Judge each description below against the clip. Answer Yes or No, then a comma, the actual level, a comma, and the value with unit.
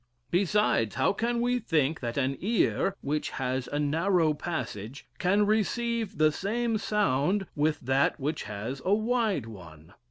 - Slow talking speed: No, average, 150 wpm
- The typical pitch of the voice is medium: Yes, medium, 160 Hz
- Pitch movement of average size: No, wide, 7.9 semitones